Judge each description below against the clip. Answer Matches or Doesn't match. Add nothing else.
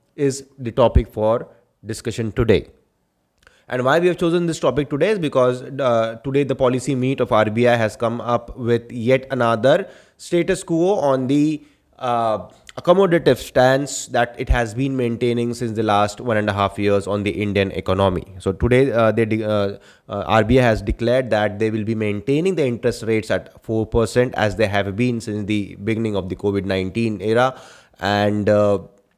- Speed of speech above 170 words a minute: Matches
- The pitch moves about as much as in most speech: Matches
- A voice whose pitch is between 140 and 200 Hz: Doesn't match